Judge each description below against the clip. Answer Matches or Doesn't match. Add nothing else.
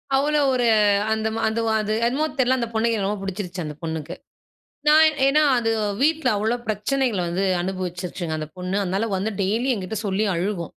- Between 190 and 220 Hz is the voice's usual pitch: Matches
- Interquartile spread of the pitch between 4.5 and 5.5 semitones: Matches